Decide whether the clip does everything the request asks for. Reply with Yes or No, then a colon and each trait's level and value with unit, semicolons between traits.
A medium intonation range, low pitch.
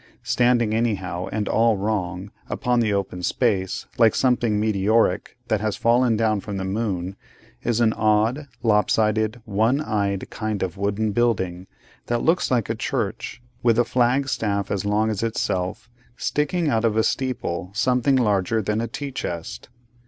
Yes: average, 3.0 semitones; low, 110 Hz